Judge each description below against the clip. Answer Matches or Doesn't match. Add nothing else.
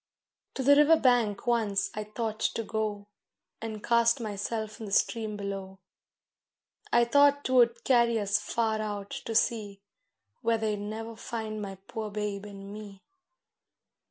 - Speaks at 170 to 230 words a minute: Doesn't match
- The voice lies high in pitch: Matches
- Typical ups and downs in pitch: Doesn't match